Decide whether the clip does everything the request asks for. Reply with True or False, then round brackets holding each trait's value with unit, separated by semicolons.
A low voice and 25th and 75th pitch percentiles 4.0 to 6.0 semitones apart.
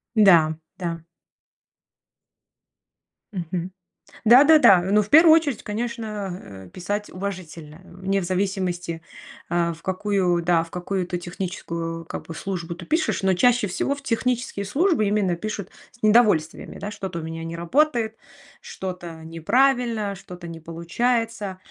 False (190 Hz; 4.3 semitones)